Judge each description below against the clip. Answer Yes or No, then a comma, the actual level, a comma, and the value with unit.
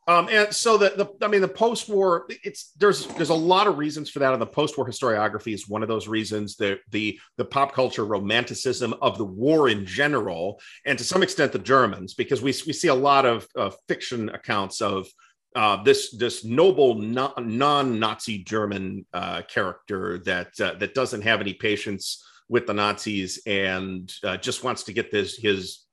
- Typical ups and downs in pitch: No, wide, 6.4 semitones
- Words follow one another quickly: No, average, 190 wpm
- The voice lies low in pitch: Yes, low, 120 Hz